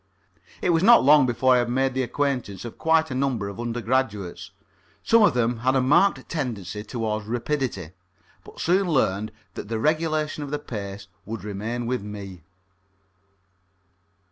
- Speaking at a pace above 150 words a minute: Yes, average, 160 wpm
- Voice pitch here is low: Yes, low, 120 Hz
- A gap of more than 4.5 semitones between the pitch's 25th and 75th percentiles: Yes, average, 5.3 semitones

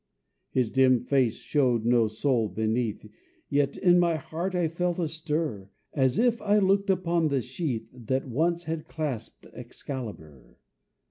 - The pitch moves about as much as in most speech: No, wide, 6.1 semitones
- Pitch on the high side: No, medium, 140 Hz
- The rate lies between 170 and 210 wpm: No, average, 145 wpm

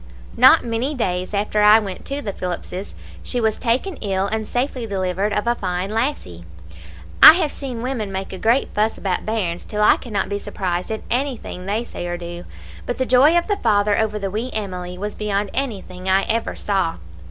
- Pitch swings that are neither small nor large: Yes, average, 4.0 semitones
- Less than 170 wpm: No, average, 200 wpm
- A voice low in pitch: No, high, 210 Hz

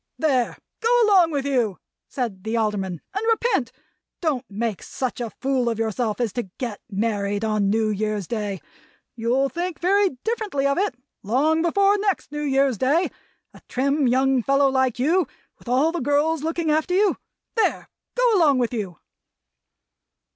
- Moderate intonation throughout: No, wide, 6.5 semitones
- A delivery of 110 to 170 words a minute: Yes, average, 160 wpm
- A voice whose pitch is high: Yes, very high, 270 Hz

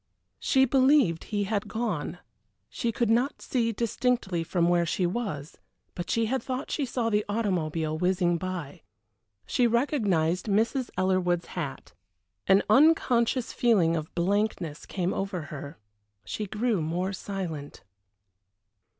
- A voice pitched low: No, high, 195 Hz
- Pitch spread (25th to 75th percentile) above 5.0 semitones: Yes, wide, 5.4 semitones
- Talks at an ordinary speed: No, slow, 130 wpm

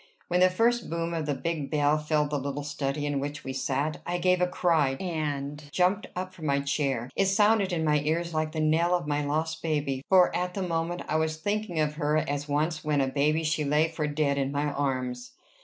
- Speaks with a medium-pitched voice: Yes, medium, 155 Hz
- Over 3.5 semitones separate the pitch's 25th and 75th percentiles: No, average, 2.9 semitones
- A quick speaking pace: Yes, fast, 225 wpm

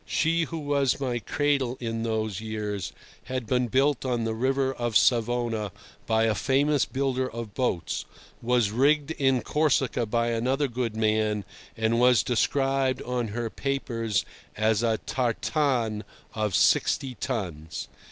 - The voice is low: Yes, low, 120 Hz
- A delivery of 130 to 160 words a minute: Yes, average, 140 wpm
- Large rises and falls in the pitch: No, average, 3.3 semitones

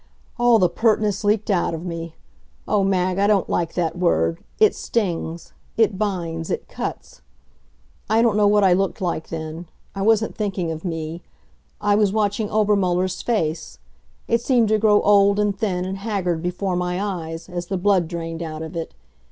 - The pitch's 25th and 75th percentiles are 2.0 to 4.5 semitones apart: Yes, average, 3.6 semitones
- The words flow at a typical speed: Yes, average, 175 wpm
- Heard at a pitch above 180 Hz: Yes, high, 190 Hz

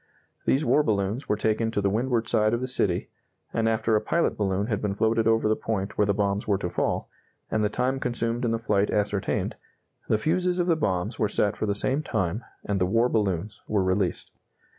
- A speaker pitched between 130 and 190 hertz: No, low, 110 Hz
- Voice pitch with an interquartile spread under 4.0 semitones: Yes, narrow, 2.6 semitones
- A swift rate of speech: Yes, fast, 220 wpm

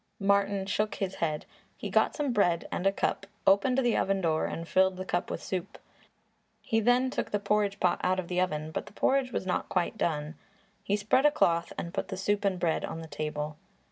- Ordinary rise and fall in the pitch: Yes, average, 3.3 semitones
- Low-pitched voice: No, high, 190 Hz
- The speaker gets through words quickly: Yes, fast, 220 wpm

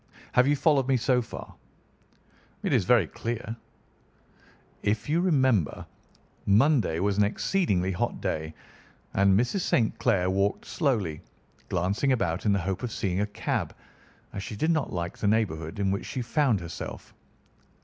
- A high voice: No, low, 105 Hz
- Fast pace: No, average, 155 wpm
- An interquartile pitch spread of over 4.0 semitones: Yes, average, 5.3 semitones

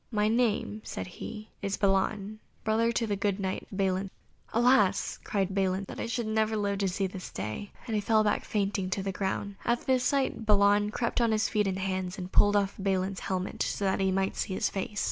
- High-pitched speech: Yes, high, 200 Hz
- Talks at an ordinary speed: No, fast, 215 wpm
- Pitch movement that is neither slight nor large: No, narrow, 2.1 semitones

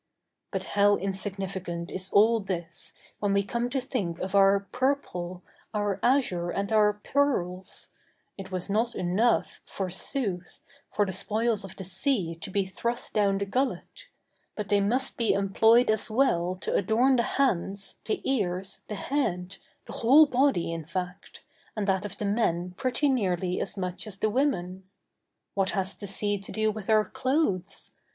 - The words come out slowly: No, average, 160 wpm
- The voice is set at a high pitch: Yes, high, 200 Hz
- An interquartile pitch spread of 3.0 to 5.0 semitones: Yes, average, 4.0 semitones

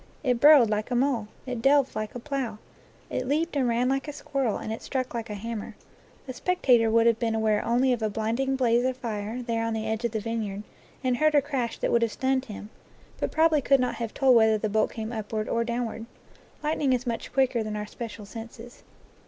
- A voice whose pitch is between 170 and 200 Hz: No, high, 235 Hz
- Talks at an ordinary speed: No, fast, 230 wpm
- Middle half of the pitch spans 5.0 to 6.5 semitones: No, average, 2.9 semitones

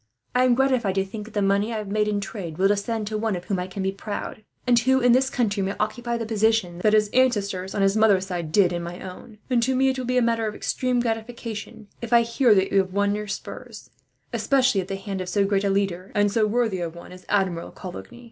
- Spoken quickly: Yes, fast, 260 wpm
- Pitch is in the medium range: No, high, 210 Hz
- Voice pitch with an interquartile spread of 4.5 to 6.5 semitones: No, average, 3.3 semitones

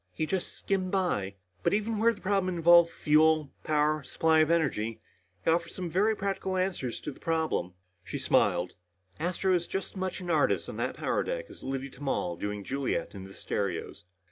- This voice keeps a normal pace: Yes, average, 185 wpm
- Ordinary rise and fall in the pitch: No, wide, 5.9 semitones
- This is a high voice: No, medium, 160 Hz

